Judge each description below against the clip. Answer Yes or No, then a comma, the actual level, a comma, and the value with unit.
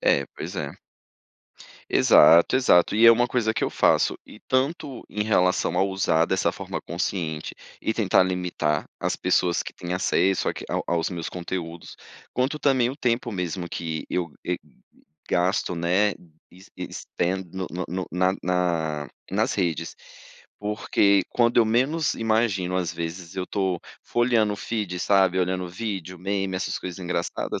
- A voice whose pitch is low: Yes, very low, 95 Hz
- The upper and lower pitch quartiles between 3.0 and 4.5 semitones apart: Yes, average, 3.7 semitones